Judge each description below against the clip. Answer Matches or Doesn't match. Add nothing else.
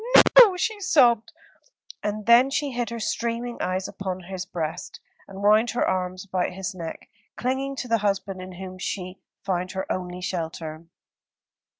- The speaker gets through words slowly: Doesn't match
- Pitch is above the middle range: Matches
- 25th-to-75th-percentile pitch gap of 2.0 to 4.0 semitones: Doesn't match